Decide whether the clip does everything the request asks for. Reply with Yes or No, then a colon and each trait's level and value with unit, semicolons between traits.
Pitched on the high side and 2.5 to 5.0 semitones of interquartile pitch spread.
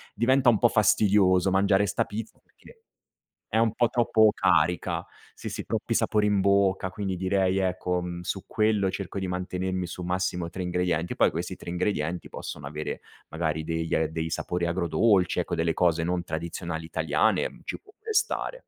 No: very low, 90 Hz; average, 2.9 semitones